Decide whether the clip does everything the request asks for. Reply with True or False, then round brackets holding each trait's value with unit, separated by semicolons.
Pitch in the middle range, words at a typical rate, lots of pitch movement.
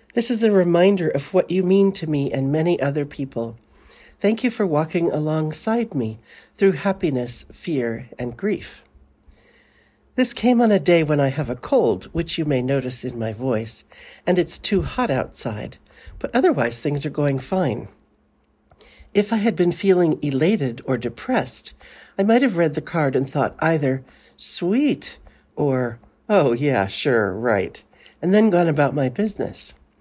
True (155 Hz; 165 wpm; 6.7 semitones)